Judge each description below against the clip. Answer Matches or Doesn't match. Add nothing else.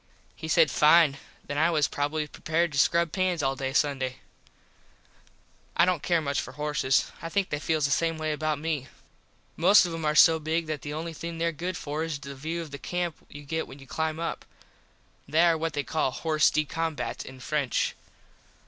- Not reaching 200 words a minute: Doesn't match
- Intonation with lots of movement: Doesn't match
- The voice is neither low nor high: Matches